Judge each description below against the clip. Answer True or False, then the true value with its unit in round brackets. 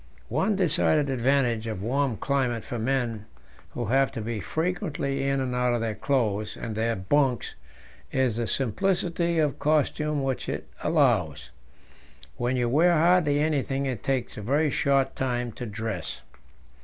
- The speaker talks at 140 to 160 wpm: True (155 wpm)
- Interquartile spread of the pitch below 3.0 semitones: False (4.0 semitones)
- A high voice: False (130 Hz)